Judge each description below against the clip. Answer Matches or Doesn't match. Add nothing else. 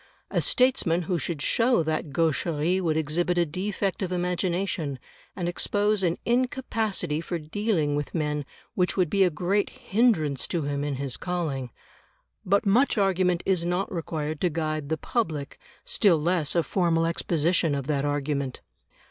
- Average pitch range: Matches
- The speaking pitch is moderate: Matches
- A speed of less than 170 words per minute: Matches